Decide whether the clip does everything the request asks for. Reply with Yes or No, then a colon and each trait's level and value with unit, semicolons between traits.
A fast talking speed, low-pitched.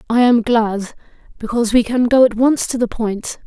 No: fast, 210 wpm; high, 230 Hz